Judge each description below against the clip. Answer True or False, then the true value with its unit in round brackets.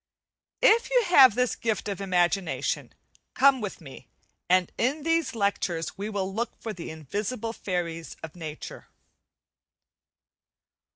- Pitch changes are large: True (6.2 semitones)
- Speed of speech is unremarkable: False (125 wpm)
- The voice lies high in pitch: True (200 Hz)